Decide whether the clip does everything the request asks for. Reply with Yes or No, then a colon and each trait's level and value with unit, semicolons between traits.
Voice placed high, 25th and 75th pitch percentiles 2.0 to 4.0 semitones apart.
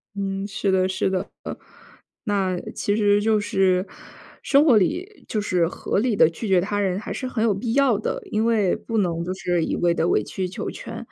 Yes: high, 200 Hz; average, 2.9 semitones